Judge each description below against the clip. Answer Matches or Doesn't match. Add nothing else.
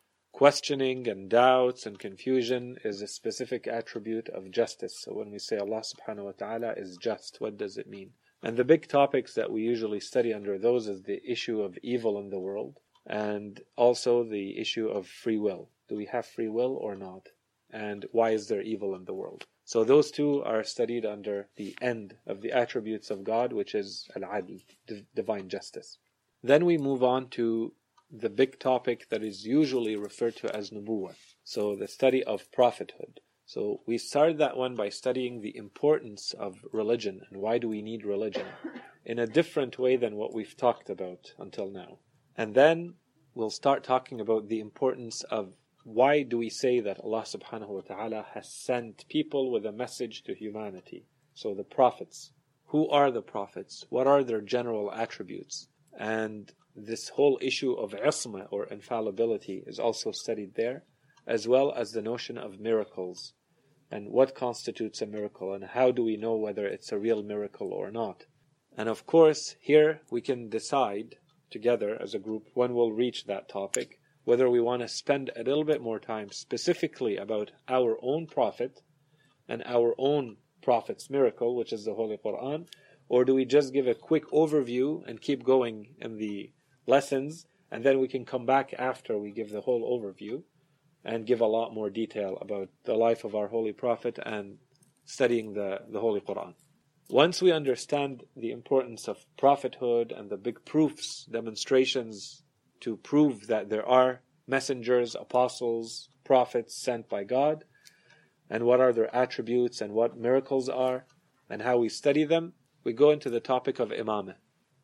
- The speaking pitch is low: Matches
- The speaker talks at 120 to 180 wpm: Matches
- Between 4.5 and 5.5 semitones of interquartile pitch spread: Doesn't match